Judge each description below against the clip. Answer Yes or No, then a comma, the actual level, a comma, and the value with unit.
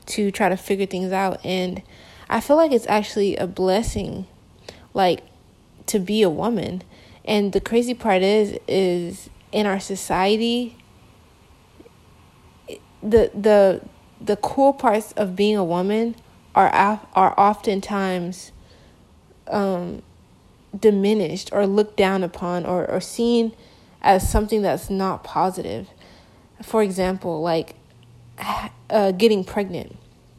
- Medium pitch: No, high, 200 Hz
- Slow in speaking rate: Yes, slow, 120 wpm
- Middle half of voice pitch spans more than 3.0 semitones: No, narrow, 2.5 semitones